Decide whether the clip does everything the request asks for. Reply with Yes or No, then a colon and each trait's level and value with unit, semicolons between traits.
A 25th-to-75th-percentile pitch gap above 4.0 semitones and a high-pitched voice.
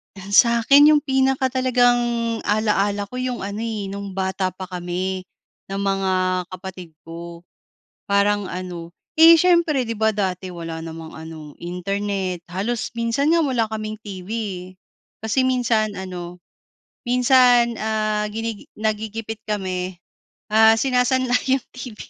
Yes: average, 4.6 semitones; high, 210 Hz